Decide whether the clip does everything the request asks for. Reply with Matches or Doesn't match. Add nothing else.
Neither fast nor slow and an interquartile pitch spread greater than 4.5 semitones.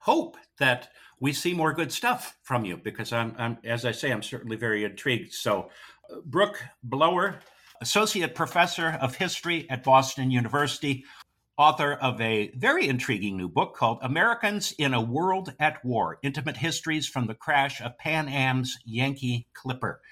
Matches